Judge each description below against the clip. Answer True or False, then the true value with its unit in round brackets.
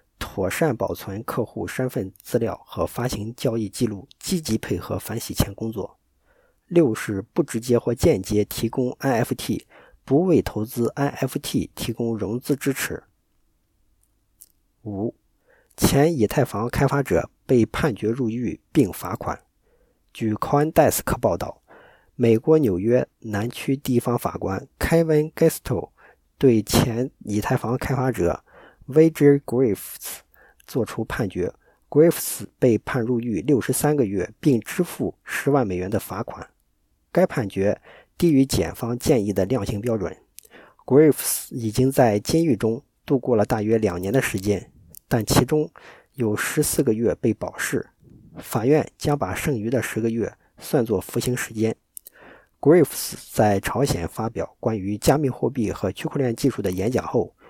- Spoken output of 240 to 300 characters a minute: True (260 characters per minute)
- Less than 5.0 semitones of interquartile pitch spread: True (4.5 semitones)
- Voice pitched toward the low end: True (120 Hz)